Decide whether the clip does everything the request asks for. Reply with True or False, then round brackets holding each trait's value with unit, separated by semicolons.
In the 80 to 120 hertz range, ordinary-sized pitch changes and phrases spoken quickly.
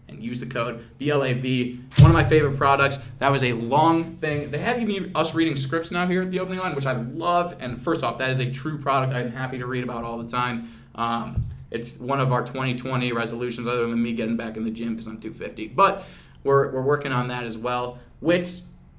False (130 Hz; 3.7 semitones; 230 wpm)